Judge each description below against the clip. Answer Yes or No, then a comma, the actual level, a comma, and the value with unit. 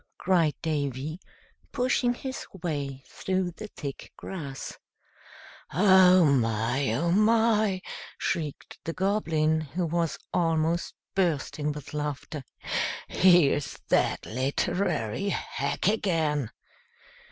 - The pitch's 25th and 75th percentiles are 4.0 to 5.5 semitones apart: Yes, average, 4.6 semitones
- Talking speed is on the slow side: Yes, slow, 95 wpm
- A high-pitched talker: No, medium, 165 Hz